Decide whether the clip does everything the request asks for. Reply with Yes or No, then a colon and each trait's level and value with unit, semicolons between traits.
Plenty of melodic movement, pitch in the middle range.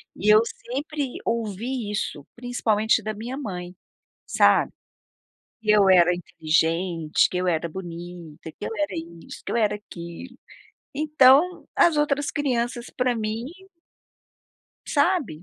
No: wide, 6.4 semitones; high, 215 Hz